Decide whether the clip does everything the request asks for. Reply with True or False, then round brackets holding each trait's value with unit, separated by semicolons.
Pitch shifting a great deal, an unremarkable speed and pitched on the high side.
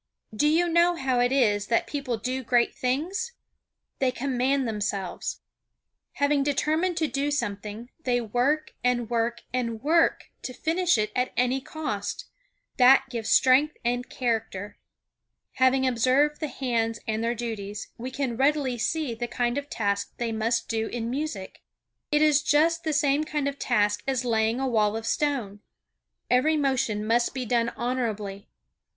False (4.0 semitones; 155 wpm; 250 Hz)